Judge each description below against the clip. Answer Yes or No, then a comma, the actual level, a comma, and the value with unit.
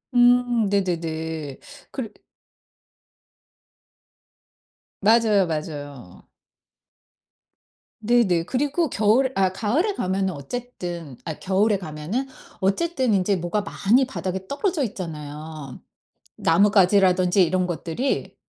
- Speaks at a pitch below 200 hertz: Yes, high, 190 Hz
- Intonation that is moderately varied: No, wide, 6.3 semitones